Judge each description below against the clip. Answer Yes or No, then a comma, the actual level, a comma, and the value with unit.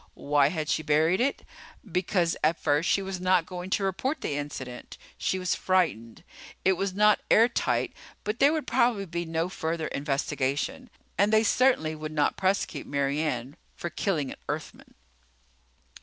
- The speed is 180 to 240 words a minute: No, average, 160 wpm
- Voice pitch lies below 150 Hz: No, medium, 175 Hz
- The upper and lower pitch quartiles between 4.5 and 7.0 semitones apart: Yes, average, 4.8 semitones